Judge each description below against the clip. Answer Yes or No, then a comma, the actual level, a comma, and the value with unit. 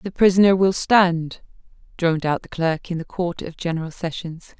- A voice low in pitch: No, medium, 175 Hz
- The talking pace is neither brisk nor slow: Yes, average, 185 wpm